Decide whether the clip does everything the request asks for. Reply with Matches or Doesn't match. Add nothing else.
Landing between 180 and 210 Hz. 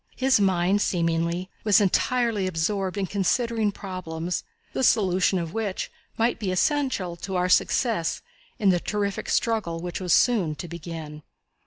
Matches